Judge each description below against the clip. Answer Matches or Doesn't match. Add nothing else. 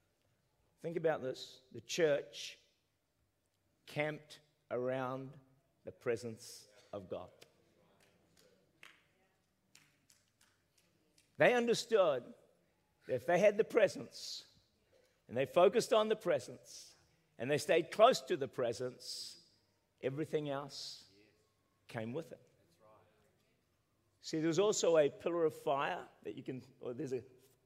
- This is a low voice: Matches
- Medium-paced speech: Doesn't match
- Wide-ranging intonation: Matches